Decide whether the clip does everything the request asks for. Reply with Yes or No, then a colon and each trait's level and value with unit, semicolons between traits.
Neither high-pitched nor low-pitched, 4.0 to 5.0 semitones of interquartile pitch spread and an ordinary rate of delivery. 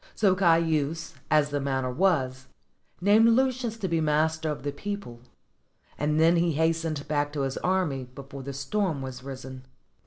Yes: medium, 155 Hz; average, 4.4 semitones; average, 160 wpm